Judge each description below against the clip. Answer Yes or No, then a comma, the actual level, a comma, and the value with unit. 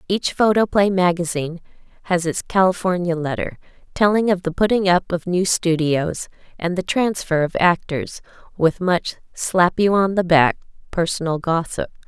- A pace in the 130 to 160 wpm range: Yes, average, 145 wpm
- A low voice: No, medium, 180 Hz